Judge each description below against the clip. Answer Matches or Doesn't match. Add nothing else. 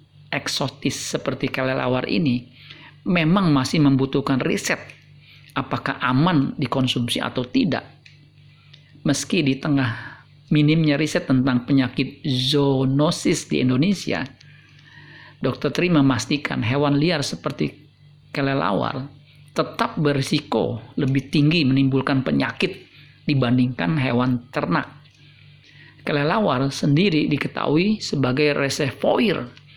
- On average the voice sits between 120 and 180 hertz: Matches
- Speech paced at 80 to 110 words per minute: Matches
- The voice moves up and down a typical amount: Doesn't match